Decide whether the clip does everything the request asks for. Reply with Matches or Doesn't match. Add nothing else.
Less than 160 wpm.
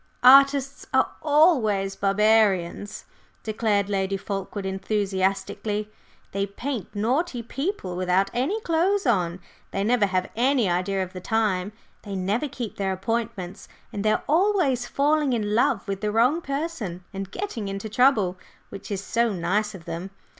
Matches